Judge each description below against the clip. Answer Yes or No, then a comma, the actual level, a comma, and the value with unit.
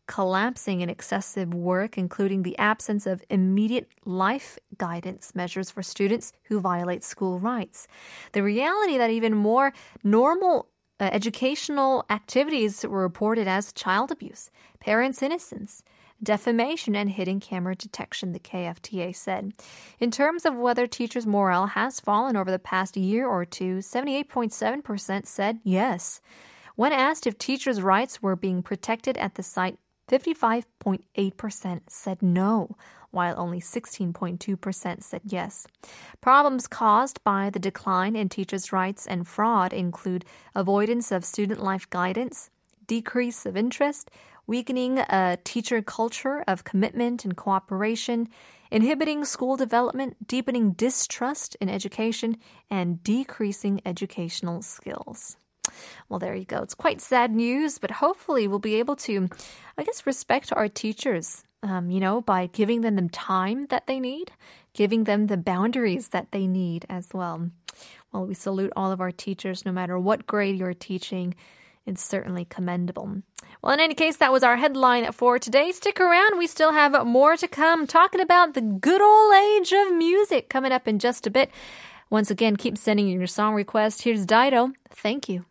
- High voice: Yes, high, 215 Hz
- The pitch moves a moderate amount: Yes, average, 4.7 semitones